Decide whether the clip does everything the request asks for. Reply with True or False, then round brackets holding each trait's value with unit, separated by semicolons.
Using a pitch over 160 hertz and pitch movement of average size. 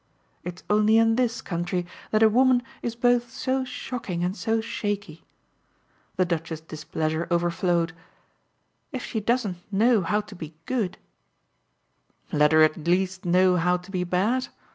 True (185 Hz; 4.7 semitones)